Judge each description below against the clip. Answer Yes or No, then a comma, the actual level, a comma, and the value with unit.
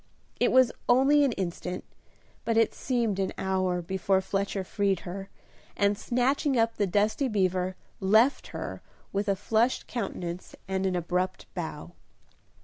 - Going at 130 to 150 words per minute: Yes, average, 140 wpm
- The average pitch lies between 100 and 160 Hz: No, high, 195 Hz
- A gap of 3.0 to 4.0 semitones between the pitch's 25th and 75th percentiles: Yes, average, 3.6 semitones